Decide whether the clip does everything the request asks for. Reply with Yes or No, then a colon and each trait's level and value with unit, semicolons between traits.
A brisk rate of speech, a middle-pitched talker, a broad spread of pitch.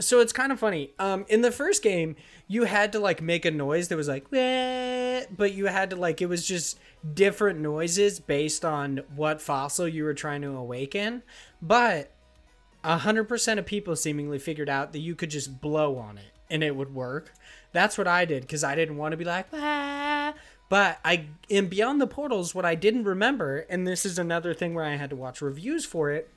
Yes: fast, 215 wpm; medium, 170 Hz; wide, 5.8 semitones